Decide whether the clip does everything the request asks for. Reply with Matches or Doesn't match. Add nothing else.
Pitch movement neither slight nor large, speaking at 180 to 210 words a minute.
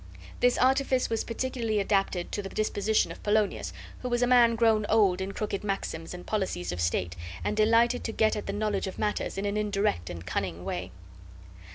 Matches